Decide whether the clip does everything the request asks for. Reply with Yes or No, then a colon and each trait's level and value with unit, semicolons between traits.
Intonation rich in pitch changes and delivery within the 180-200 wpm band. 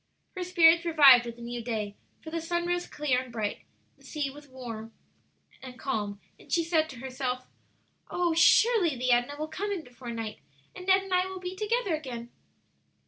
Yes: wide, 6.2 semitones; average, 185 wpm